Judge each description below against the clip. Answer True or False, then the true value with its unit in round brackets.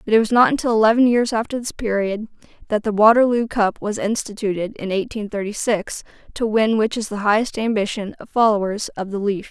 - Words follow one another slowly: False (200 wpm)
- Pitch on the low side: False (215 Hz)